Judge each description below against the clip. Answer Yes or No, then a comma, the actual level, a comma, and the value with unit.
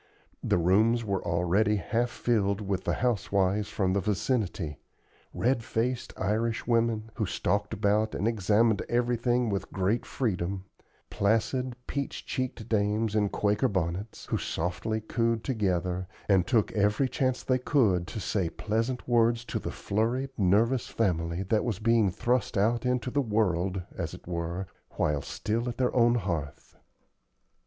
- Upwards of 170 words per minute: No, average, 150 wpm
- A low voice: Yes, low, 110 Hz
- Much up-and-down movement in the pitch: No, average, 3.6 semitones